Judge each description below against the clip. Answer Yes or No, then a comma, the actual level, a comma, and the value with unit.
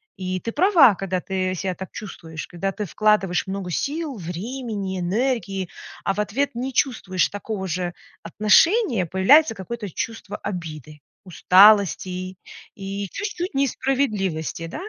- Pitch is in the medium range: No, high, 195 Hz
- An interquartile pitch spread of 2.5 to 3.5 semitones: No, average, 4.4 semitones